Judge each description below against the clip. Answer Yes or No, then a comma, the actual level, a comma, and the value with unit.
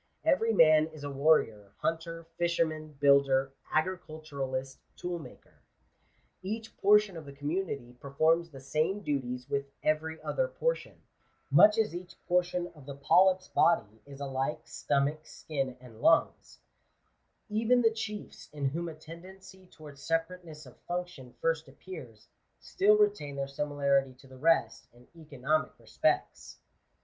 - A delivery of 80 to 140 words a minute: Yes, slow, 135 wpm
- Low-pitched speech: No, medium, 155 Hz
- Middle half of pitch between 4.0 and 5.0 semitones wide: Yes, average, 4.4 semitones